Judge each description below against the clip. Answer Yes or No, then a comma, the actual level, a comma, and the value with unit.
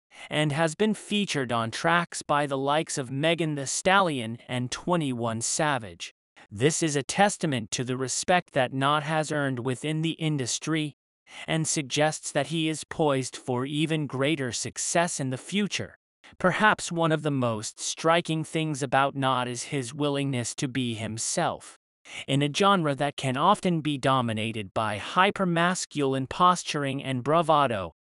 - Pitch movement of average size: Yes, average, 4.2 semitones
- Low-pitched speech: No, medium, 145 Hz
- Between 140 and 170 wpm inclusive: Yes, average, 155 wpm